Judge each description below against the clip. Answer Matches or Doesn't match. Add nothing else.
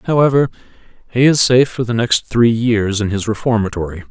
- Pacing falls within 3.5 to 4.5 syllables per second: Doesn't match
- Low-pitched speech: Matches